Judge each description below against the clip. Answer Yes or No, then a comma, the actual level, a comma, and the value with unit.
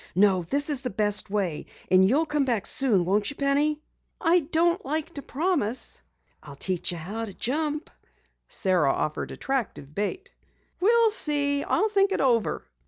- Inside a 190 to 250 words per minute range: No, average, 165 wpm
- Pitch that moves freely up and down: Yes, wide, 7.6 semitones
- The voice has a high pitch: Yes, very high, 270 Hz